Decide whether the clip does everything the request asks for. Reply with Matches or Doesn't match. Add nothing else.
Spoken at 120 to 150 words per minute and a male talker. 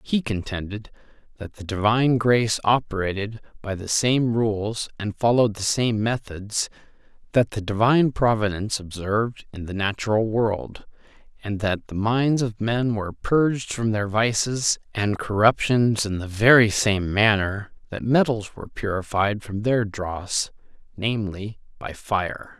Matches